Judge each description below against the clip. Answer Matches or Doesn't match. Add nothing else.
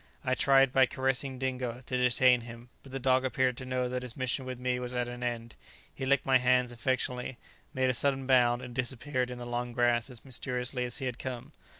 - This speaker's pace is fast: Matches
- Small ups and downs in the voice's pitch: Matches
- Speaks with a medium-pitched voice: Doesn't match